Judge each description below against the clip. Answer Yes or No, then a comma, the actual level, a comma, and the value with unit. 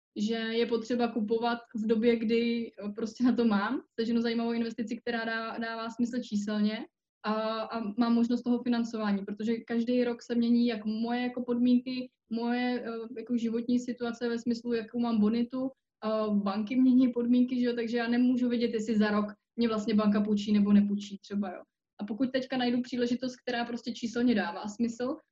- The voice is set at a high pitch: Yes, high, 235 Hz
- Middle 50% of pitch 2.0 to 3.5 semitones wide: No, narrow, 1.5 semitones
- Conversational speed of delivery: No, fast, 175 wpm